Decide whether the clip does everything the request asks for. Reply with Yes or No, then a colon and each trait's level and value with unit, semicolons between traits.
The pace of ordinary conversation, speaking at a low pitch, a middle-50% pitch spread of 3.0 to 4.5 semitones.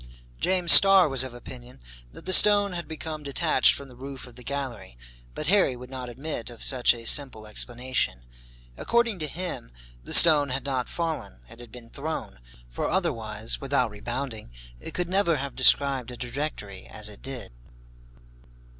No: average, 170 wpm; low, 130 Hz; average, 4.9 semitones